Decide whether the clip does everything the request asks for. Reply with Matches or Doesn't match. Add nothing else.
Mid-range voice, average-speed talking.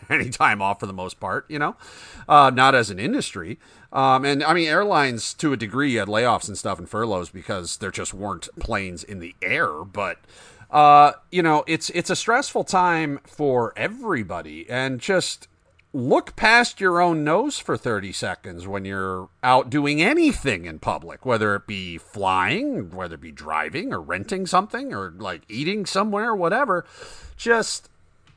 Matches